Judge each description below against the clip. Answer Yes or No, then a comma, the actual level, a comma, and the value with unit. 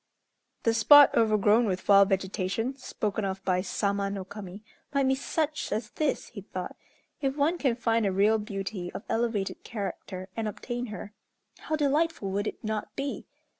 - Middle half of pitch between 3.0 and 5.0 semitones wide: Yes, average, 3.9 semitones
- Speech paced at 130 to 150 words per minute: No, average, 170 wpm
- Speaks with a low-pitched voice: No, high, 215 Hz